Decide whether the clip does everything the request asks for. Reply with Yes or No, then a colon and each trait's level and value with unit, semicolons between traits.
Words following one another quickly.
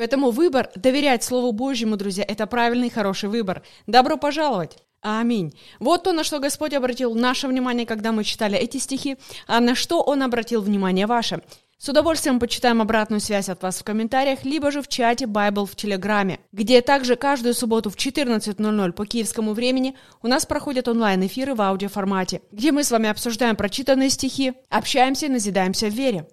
Yes: fast, 175 wpm